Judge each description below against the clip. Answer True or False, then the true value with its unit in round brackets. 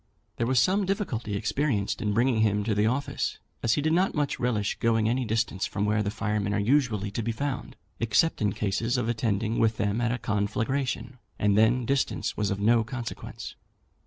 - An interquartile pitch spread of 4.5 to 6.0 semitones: False (3.4 semitones)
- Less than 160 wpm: False (195 wpm)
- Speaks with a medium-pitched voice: False (115 Hz)